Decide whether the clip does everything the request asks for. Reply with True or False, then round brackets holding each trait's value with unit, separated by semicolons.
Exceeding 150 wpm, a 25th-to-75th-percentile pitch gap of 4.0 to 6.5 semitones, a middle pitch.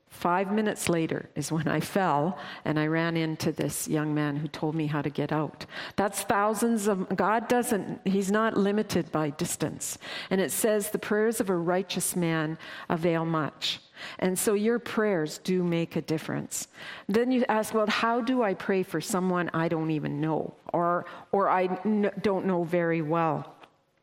True (180 wpm; 4.6 semitones; 180 Hz)